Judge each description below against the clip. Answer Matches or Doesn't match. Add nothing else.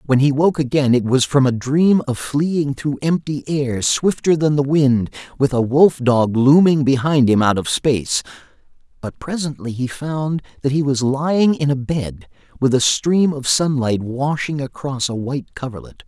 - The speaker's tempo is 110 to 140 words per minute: Doesn't match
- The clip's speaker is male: Matches